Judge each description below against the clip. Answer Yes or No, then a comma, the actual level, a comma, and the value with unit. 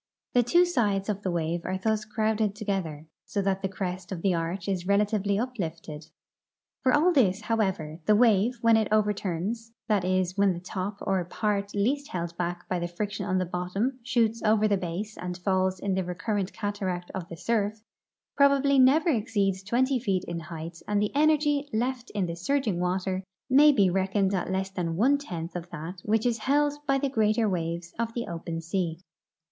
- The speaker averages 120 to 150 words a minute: No, average, 200 wpm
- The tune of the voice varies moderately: Yes, average, 4.2 semitones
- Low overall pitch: No, high, 200 Hz